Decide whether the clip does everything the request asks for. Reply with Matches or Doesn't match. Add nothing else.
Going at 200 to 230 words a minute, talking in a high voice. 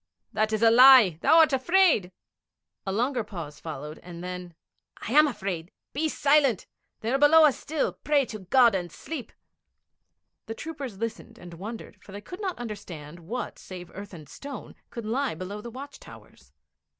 Doesn't match